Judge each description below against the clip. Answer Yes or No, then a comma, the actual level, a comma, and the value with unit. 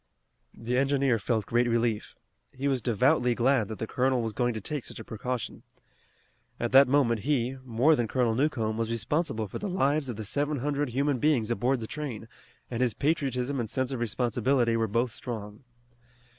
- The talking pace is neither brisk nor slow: Yes, average, 185 wpm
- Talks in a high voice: No, low, 125 Hz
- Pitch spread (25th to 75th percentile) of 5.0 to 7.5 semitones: No, average, 3.3 semitones